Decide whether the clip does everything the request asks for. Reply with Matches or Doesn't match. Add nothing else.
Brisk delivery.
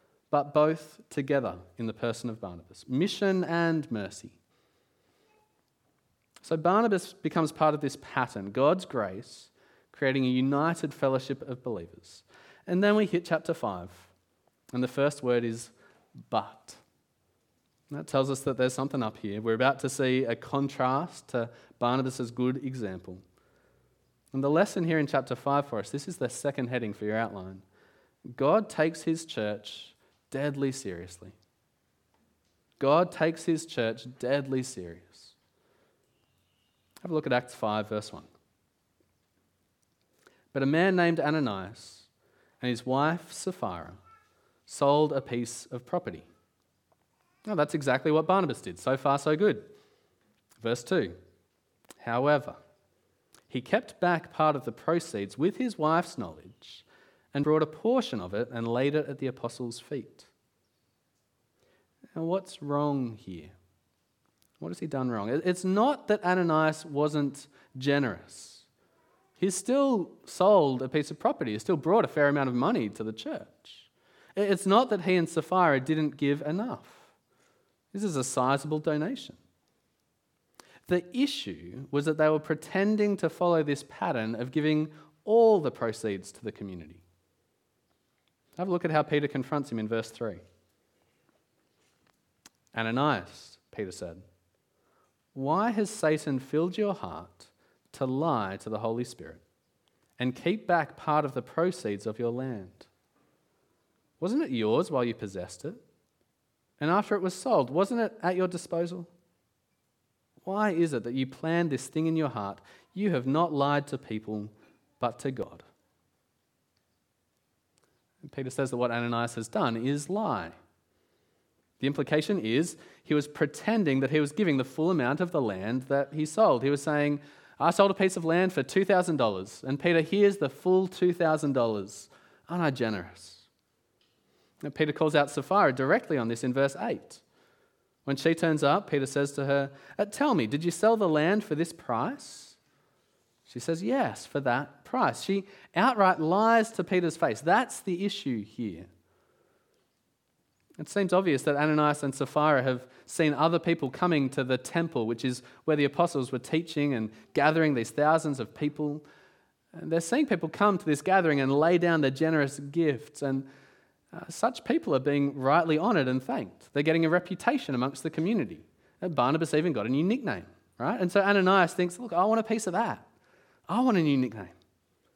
Doesn't match